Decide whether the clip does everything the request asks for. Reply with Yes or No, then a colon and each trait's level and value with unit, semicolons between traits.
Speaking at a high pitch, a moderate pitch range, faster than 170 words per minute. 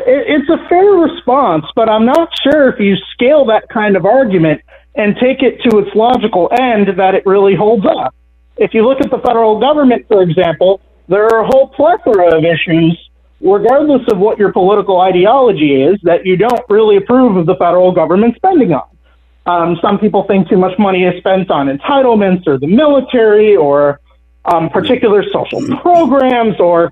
No: high, 210 Hz; wide, 5.8 semitones; average, 180 wpm